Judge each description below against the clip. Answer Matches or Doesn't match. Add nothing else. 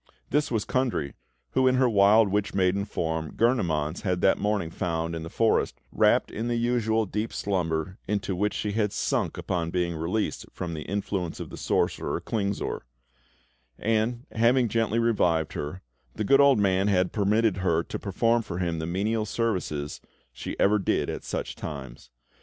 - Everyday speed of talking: Matches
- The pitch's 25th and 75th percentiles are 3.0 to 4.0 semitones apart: Doesn't match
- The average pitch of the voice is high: Doesn't match